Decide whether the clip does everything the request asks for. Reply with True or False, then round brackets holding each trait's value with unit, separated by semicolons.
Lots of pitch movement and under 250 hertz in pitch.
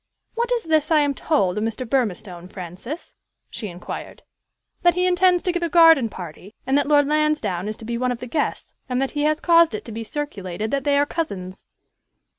False (6.9 semitones; 275 Hz)